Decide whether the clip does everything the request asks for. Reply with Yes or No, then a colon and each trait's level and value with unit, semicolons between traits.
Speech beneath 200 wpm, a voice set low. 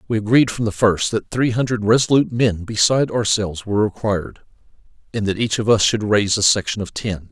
No: fast, 205 wpm; low, 110 Hz